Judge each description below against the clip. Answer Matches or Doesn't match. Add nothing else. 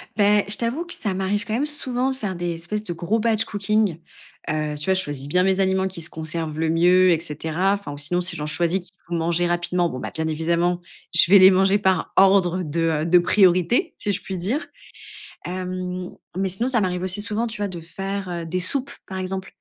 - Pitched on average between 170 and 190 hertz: Matches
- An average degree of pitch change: Matches